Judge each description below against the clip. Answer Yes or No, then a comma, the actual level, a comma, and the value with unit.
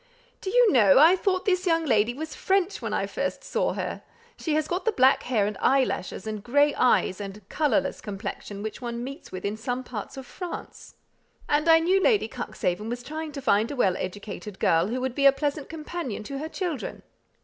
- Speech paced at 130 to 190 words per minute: No, fast, 205 wpm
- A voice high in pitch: Yes, very high, 265 Hz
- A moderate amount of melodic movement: No, wide, 6.9 semitones